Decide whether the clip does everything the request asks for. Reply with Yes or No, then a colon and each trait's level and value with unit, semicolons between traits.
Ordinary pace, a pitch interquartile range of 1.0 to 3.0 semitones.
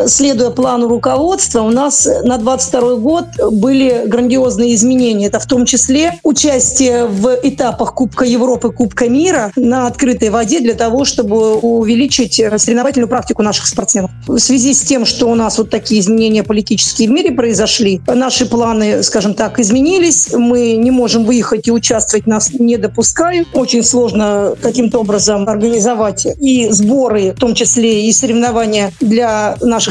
Yes: average, 150 wpm; narrow, 2.4 semitones